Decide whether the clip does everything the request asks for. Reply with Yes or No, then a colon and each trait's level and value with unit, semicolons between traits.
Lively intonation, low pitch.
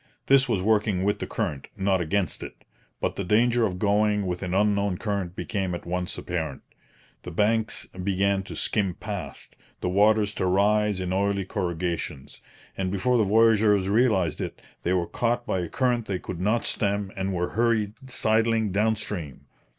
No: average, 3.0 semitones; low, 100 Hz